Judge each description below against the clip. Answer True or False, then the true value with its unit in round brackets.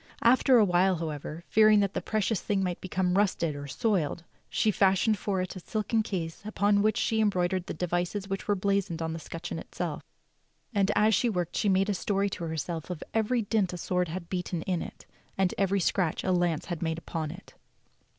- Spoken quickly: True (210 wpm)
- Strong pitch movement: False (3.1 semitones)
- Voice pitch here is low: False (185 Hz)